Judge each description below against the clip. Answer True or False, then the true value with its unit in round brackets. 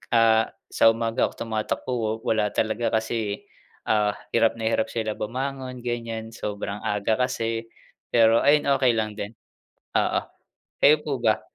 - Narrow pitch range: True (1.6 semitones)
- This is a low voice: True (115 Hz)